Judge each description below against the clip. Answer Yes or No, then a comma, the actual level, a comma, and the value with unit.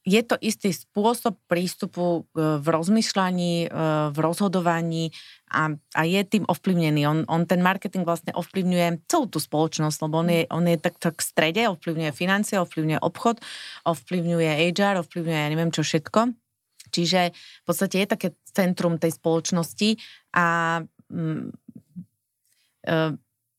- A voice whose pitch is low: No, medium, 170 Hz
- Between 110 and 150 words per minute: Yes, average, 135 wpm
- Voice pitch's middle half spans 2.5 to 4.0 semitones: Yes, average, 3.0 semitones